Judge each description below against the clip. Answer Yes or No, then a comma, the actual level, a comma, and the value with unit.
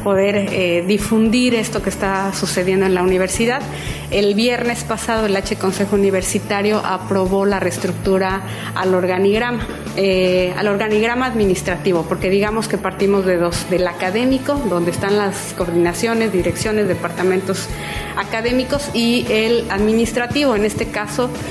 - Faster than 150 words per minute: No, average, 130 wpm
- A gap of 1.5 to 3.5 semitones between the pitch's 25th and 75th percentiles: Yes, average, 3.0 semitones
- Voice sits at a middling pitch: No, high, 200 Hz